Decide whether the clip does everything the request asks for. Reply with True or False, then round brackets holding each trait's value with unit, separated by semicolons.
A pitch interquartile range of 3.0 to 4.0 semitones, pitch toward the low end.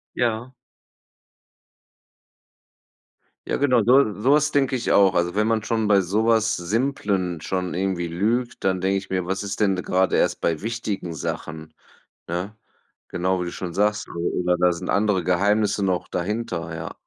True (3.6 semitones; 95 Hz)